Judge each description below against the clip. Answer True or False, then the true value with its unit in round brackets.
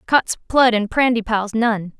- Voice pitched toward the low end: False (225 Hz)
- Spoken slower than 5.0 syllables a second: True (4.1 syllables/s)